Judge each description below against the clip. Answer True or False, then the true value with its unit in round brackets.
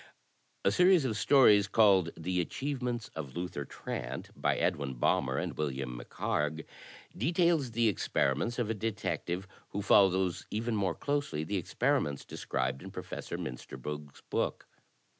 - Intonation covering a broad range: True (8.0 semitones)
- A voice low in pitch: True (95 Hz)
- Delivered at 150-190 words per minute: False (135 wpm)